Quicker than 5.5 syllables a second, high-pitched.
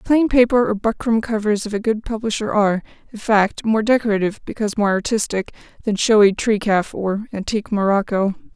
Yes: 5.8 syllables/s; high, 215 Hz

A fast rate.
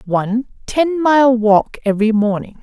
No: slow, 135 wpm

